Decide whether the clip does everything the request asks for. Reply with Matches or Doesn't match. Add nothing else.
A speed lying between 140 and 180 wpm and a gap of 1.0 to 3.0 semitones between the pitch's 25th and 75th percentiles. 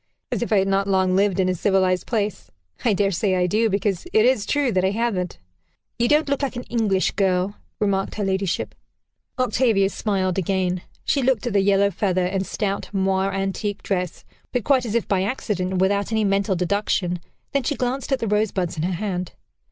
Doesn't match